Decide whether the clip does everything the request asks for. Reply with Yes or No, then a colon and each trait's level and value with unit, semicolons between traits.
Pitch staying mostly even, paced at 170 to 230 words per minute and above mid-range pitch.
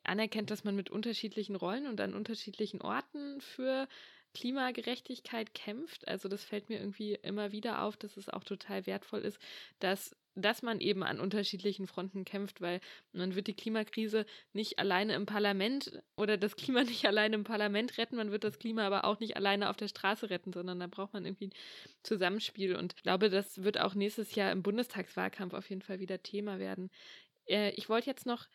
Yes: narrow, 2.1 semitones; fast, 190 wpm; high, 210 Hz